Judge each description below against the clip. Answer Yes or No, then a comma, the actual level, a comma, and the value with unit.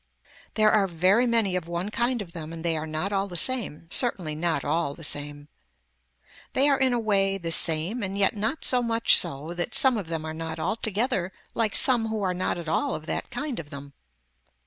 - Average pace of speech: No, fast, 215 wpm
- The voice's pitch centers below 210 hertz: Yes, high, 190 Hz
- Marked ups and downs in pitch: Yes, wide, 5.8 semitones